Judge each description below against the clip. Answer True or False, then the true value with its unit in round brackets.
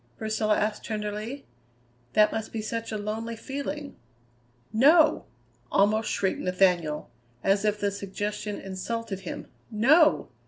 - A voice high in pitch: True (215 Hz)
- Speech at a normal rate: False (120 wpm)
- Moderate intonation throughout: False (2.2 semitones)